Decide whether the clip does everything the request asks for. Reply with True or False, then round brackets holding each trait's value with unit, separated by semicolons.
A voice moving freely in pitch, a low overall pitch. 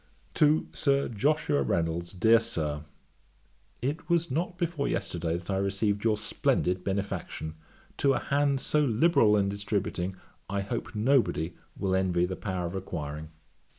True (7.5 semitones; 100 Hz)